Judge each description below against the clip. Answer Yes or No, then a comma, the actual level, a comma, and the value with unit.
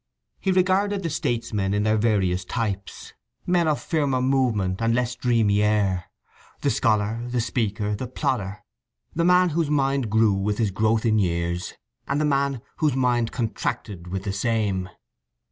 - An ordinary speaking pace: Yes, average, 160 wpm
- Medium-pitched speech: No, low, 115 Hz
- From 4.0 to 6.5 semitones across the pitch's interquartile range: Yes, average, 5.1 semitones